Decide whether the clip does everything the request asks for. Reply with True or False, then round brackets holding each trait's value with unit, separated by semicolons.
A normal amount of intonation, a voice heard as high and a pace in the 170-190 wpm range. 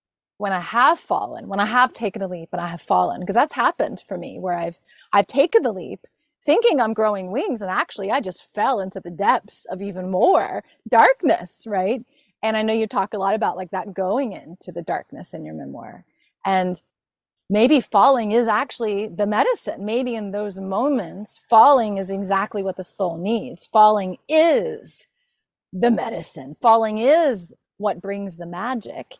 True (4.0 semitones; 205 Hz; 180 wpm)